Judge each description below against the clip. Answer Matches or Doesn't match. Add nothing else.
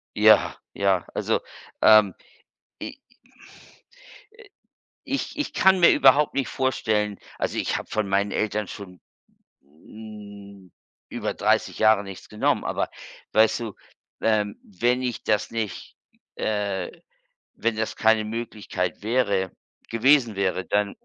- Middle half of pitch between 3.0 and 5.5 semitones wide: Doesn't match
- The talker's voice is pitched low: Matches